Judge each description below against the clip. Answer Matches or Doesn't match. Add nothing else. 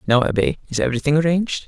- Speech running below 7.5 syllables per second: Doesn't match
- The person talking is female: Doesn't match